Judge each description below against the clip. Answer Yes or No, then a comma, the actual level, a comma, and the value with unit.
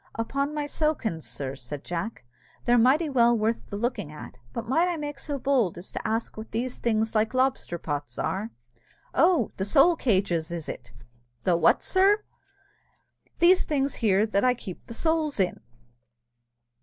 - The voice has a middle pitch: No, high, 230 Hz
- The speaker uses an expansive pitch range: Yes, wide, 6.8 semitones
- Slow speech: No, average, 170 wpm